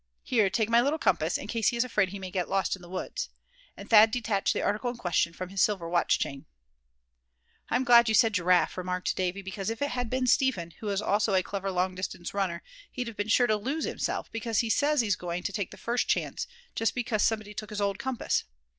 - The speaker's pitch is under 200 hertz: No, high, 210 Hz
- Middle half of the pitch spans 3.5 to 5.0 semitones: Yes, average, 4.0 semitones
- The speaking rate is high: Yes, fast, 240 wpm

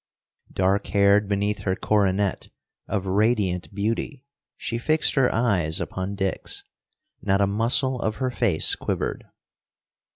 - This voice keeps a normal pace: No, slow, 125 wpm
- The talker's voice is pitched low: Yes, low, 100 Hz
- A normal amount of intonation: Yes, average, 3.3 semitones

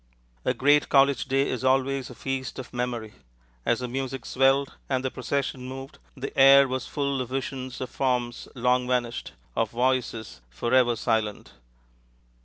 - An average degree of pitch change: No, narrow, 1.7 semitones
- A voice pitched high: No, low, 130 Hz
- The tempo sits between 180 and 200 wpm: No, average, 155 wpm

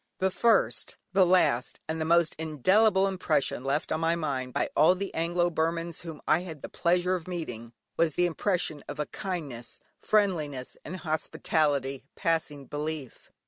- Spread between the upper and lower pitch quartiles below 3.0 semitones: No, average, 3.4 semitones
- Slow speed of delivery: No, average, 160 wpm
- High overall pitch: No, medium, 160 Hz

